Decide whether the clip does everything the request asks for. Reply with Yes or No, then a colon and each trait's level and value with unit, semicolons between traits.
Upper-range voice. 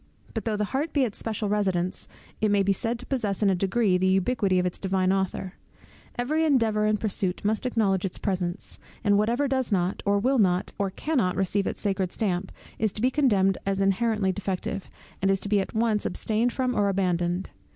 Yes: high, 200 Hz